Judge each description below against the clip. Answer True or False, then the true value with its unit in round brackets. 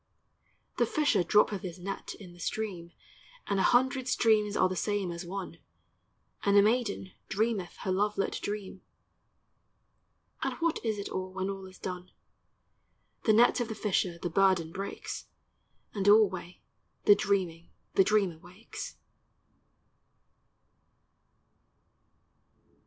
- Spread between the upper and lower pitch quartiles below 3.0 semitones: True (2.5 semitones)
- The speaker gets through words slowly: True (130 wpm)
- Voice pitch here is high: True (195 Hz)